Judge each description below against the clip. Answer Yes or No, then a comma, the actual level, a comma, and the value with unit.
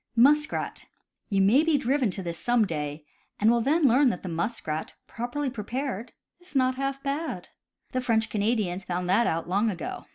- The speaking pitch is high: Yes, high, 235 Hz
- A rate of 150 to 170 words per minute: No, average, 180 wpm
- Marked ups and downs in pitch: Yes, wide, 6.1 semitones